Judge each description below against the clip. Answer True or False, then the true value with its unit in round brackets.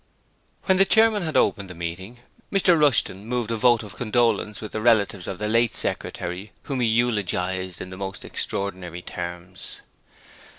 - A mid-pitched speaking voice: False (105 Hz)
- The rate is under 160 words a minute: False (165 wpm)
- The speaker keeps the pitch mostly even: False (4.6 semitones)